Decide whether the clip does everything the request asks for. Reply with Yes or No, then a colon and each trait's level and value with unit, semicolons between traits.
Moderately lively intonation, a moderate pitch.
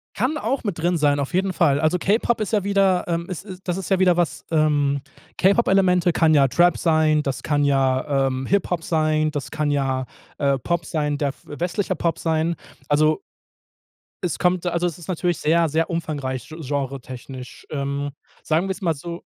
Yes: average, 3.7 semitones; medium, 160 Hz